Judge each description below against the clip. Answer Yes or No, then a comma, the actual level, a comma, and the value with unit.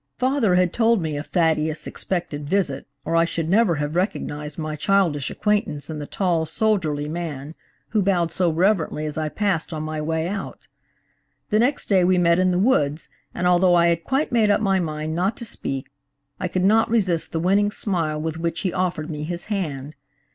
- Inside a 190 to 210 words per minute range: Yes, average, 200 wpm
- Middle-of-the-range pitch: Yes, medium, 170 Hz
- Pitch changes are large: No, average, 4.0 semitones